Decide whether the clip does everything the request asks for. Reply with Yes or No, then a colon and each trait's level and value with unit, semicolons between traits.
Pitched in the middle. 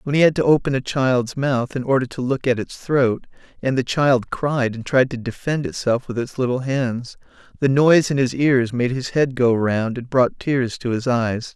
No: low, 130 Hz